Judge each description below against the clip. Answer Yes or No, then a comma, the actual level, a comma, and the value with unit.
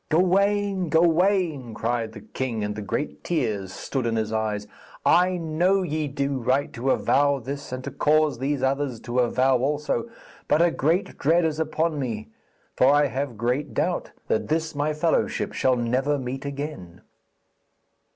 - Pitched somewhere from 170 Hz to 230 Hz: No, medium, 140 Hz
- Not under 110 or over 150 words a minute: No, average, 160 wpm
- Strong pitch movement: No, average, 4.4 semitones